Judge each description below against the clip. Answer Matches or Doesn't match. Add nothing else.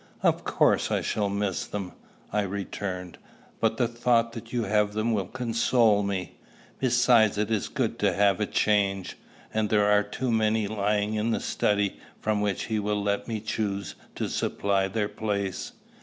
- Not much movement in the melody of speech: Matches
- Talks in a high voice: Doesn't match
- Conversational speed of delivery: Matches